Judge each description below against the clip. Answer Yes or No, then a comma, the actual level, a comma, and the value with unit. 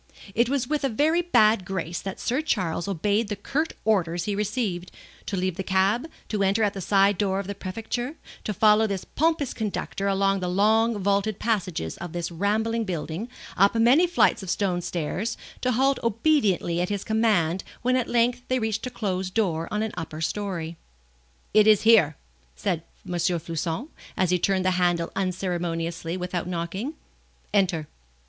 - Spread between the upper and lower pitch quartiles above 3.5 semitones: Yes, average, 4.1 semitones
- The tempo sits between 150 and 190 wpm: Yes, average, 175 wpm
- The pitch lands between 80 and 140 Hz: No, high, 200 Hz